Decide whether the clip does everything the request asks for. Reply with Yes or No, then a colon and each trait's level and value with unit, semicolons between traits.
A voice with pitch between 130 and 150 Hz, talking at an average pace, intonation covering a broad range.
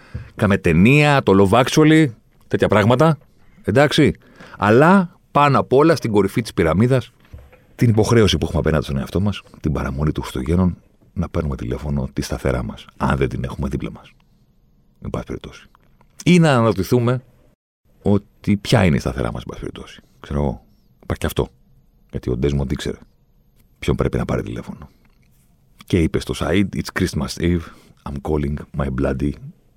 No: very low, 85 Hz; average, 160 wpm; wide, 8.7 semitones